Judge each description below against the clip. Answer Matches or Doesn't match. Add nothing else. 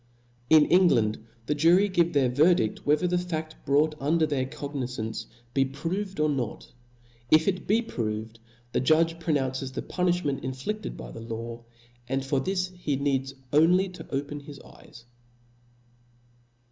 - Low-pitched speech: Doesn't match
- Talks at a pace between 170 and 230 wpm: Doesn't match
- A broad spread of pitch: Doesn't match